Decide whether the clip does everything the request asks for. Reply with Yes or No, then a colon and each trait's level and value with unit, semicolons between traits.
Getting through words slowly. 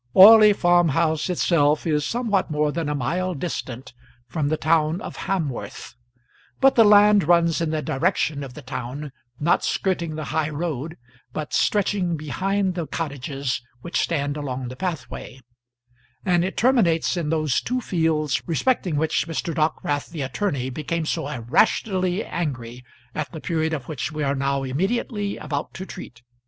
No: average, 160 wpm